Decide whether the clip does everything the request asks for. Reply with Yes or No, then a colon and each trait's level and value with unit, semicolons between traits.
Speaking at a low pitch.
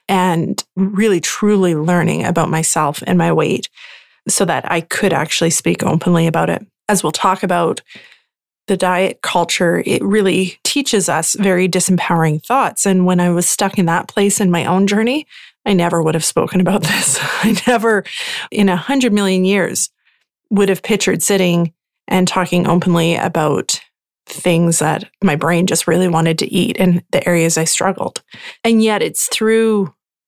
No: medium, 185 Hz